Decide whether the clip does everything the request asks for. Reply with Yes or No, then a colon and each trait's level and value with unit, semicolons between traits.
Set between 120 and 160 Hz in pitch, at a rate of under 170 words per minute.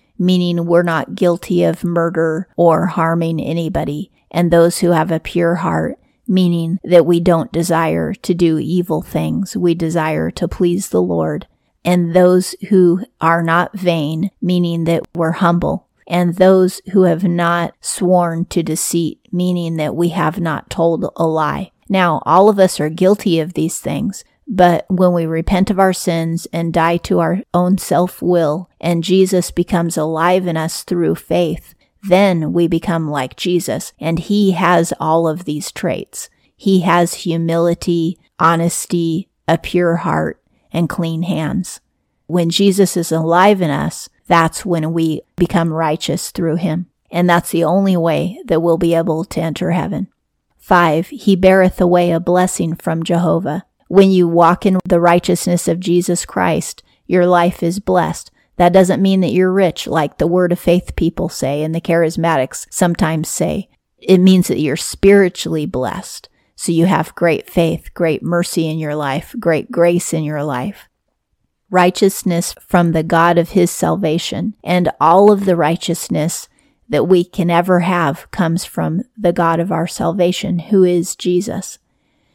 No: medium, 175 Hz; average, 160 wpm